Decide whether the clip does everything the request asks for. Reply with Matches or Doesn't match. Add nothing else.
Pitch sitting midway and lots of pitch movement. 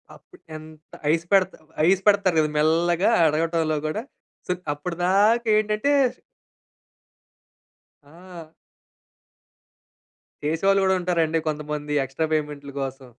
Doesn't match